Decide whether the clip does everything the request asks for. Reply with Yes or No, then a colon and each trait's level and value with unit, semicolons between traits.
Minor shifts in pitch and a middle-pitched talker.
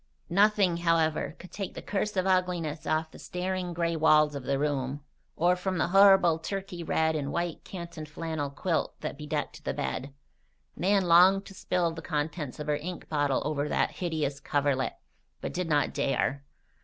No: average, 3.5 semitones; medium, 165 Hz